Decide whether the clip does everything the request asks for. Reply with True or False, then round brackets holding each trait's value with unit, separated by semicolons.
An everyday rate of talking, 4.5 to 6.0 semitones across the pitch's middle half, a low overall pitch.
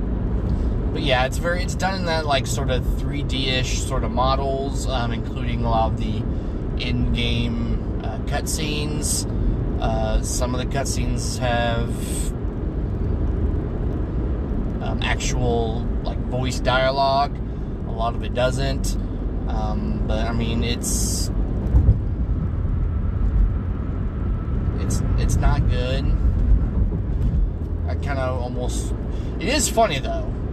False (110 wpm; 5.2 semitones; 100 Hz)